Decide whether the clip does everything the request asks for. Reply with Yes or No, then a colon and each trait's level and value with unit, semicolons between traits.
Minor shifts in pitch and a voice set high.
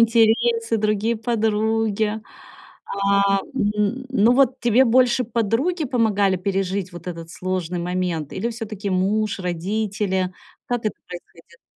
No: average, 3.5 semitones; high, 210 Hz